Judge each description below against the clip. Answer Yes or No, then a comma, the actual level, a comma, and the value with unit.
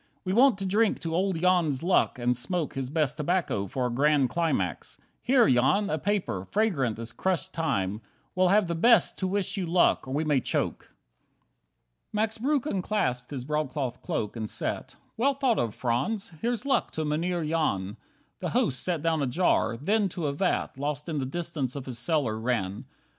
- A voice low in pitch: No, medium, 155 Hz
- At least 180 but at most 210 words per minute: Yes, average, 190 wpm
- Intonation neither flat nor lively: No, wide, 6.9 semitones